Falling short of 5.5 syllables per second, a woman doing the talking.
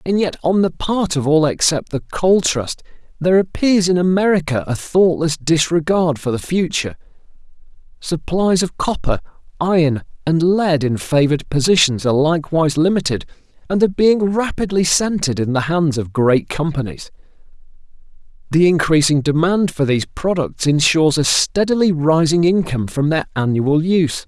No: 5.1 syllables/s; male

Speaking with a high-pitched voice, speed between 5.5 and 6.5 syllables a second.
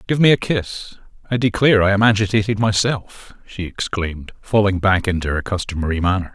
No: low, 100 Hz; 5.6 syllables/s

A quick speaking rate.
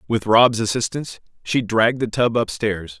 No: average, 160 wpm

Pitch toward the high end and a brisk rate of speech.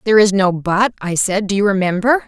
Yes: high, 200 Hz; fast, 235 wpm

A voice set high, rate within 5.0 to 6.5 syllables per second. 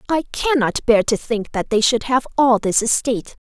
No: high, 240 Hz; 4.8 syllables/s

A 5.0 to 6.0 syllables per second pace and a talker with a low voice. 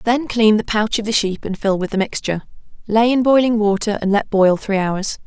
No: 5.4 syllables/s; high, 210 Hz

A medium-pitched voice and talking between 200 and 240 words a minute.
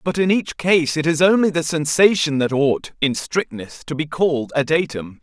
Yes: medium, 155 Hz; fast, 205 wpm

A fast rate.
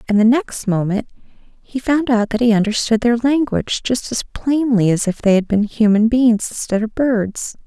No: average, 195 wpm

